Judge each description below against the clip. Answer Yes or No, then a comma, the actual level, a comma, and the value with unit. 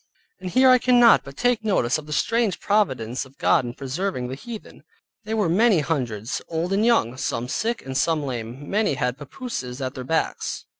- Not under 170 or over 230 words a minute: Yes, average, 195 wpm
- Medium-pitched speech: Yes, medium, 155 Hz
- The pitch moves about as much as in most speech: No, wide, 9.0 semitones